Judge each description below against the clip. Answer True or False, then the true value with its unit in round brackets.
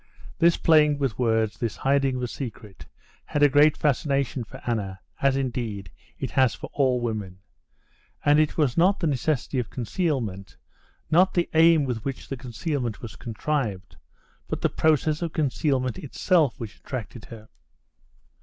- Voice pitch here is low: True (130 Hz)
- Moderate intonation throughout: True (4.8 semitones)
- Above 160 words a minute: False (155 wpm)